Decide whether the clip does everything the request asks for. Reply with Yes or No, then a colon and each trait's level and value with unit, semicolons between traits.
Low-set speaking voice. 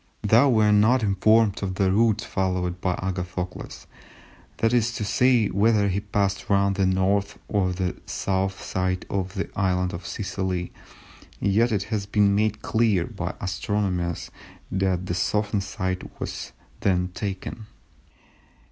Yes: low, 100 Hz